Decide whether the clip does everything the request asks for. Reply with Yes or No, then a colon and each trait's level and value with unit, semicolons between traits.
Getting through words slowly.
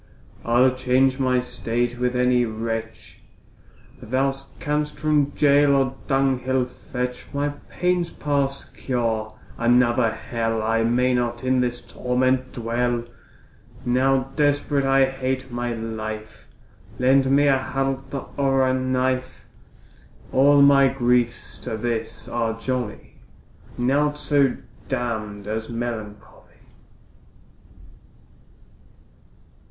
Yes: slow, 105 wpm